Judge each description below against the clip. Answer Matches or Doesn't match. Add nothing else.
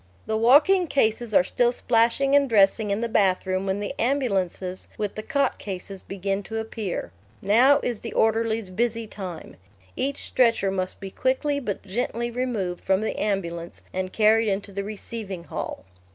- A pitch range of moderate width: Matches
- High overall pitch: Matches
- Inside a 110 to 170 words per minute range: Matches